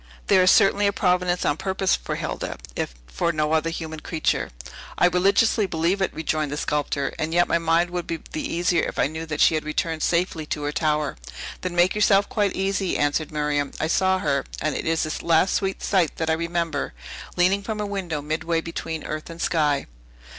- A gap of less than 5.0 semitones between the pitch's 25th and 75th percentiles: Yes, average, 3.1 semitones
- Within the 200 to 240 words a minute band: Yes, fast, 205 wpm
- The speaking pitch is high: No, medium, 165 Hz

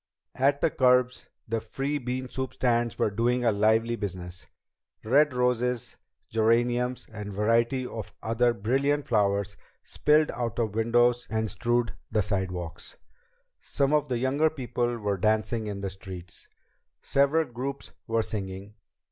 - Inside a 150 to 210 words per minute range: No, average, 140 wpm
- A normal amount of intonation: Yes, average, 3.1 semitones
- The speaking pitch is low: Yes, low, 120 Hz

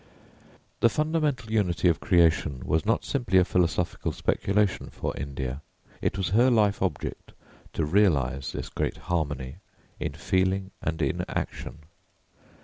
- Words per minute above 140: No, slow, 135 wpm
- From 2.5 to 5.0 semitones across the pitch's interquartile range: No, wide, 5.4 semitones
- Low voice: Yes, very low, 90 Hz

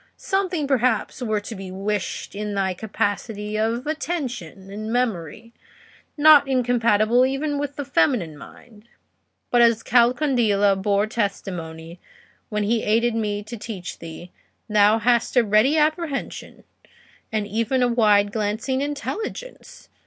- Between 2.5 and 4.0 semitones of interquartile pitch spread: Yes, average, 3.7 semitones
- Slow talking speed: Yes, slow, 130 wpm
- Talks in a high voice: Yes, high, 225 Hz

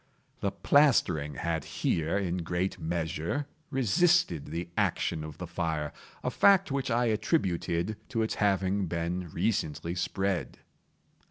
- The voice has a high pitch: No, very low, 90 Hz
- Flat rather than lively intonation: No, average, 5.1 semitones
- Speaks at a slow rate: Yes, slow, 120 wpm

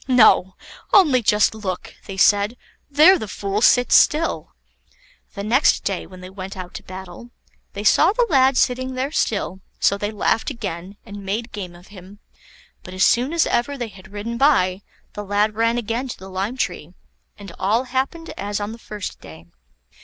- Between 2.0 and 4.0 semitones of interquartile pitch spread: No, average, 4.5 semitones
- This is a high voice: Yes, high, 210 Hz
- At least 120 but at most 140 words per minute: No, average, 185 wpm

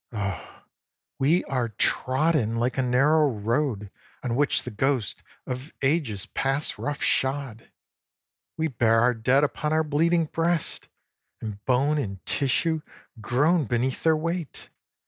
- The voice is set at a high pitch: No, low, 135 Hz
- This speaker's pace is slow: Yes, slow, 130 wpm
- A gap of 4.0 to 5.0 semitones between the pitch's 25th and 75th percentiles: Yes, average, 4.6 semitones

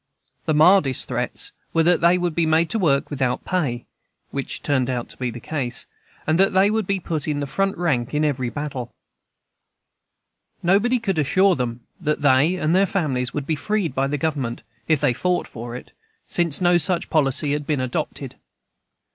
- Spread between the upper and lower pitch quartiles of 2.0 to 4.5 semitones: No, average, 5.0 semitones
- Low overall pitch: No, medium, 150 Hz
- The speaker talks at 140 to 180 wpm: No, average, 190 wpm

